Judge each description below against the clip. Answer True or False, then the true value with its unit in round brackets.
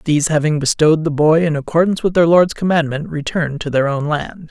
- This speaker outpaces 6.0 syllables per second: True (6.2 syllables/s)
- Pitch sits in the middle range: True (155 Hz)